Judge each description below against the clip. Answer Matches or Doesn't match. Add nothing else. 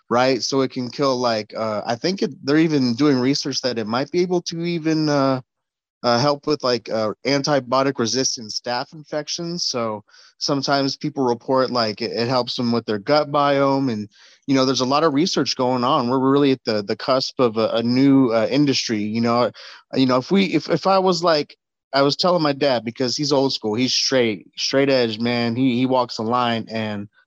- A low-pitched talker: Matches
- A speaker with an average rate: Doesn't match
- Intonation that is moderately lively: Matches